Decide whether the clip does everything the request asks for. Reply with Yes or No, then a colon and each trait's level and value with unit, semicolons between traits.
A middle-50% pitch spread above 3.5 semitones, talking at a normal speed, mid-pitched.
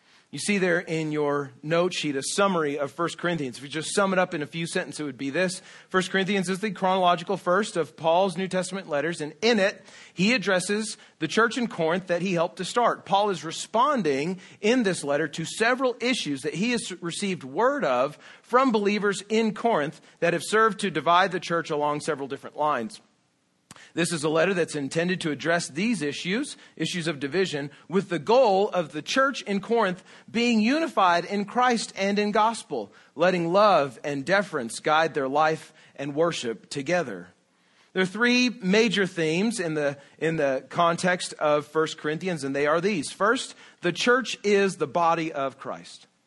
Yes: average, 4.7 semitones; average, 185 wpm; medium, 180 Hz